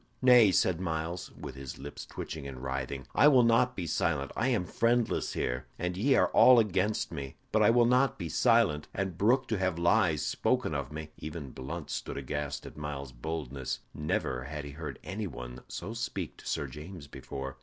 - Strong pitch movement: Yes, wide, 7.7 semitones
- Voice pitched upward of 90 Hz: No, very low, 80 Hz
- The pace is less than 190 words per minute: No, average, 195 wpm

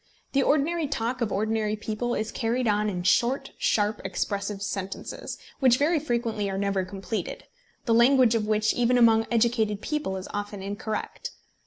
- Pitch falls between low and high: No, high, 220 Hz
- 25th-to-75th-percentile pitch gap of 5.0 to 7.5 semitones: No, average, 3.0 semitones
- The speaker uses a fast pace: No, average, 160 wpm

